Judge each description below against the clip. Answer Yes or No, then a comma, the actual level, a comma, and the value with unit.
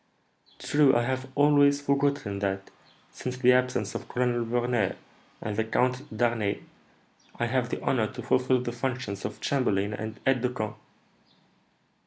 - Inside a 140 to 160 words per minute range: Yes, average, 150 wpm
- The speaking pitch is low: Yes, low, 125 Hz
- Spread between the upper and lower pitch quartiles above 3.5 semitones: No, average, 2.9 semitones